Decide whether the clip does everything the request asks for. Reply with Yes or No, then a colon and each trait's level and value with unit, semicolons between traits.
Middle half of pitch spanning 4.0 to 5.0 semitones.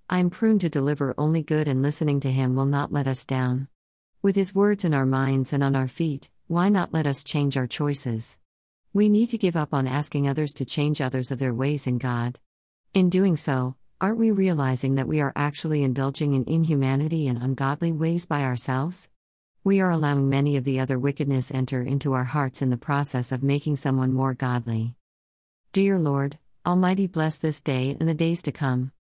No: average, 3.3 semitones